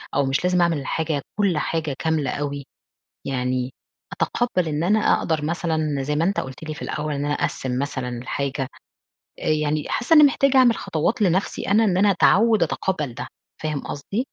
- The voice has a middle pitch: Yes, medium, 155 Hz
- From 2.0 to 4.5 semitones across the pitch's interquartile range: No, average, 4.9 semitones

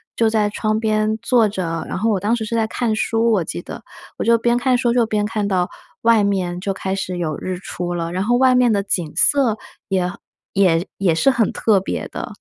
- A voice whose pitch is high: Yes, high, 210 Hz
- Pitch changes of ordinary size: Yes, average, 3.7 semitones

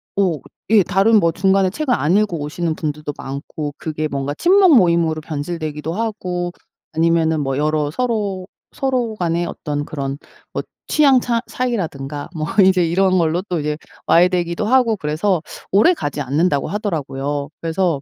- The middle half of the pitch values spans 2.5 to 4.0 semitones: No, average, 5.1 semitones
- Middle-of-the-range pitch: Yes, medium, 170 Hz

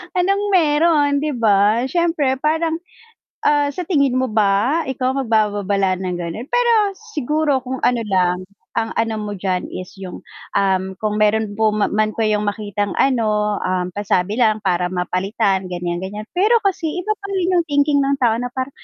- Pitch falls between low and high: No, high, 220 Hz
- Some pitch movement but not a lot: No, wide, 6.5 semitones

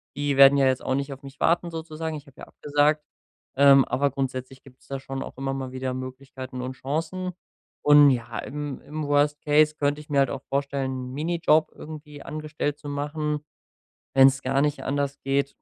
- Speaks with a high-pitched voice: No, medium, 140 Hz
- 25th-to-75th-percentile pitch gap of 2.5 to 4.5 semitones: No, narrow, 1.9 semitones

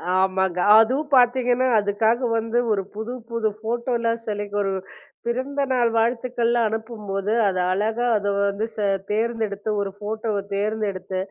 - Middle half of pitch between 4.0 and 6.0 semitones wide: No, average, 2.8 semitones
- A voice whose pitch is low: No, high, 220 Hz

